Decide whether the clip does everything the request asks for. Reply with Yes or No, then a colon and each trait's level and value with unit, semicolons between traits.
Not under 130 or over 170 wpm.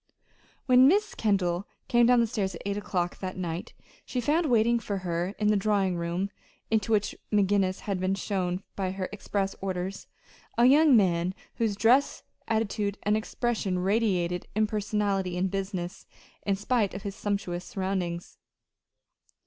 Yes: average, 150 wpm